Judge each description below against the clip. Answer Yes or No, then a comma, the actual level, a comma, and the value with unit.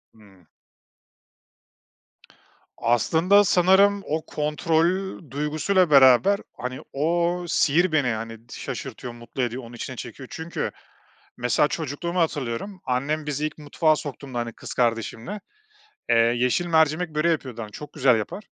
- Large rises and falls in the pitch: Yes, wide, 5.7 semitones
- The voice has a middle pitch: Yes, medium, 150 Hz